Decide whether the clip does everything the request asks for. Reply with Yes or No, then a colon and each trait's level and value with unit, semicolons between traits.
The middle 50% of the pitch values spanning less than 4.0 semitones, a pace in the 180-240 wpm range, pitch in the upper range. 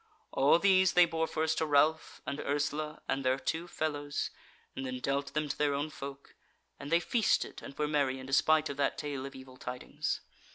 No: narrow, 2.4 semitones; average, 200 wpm; medium, 145 Hz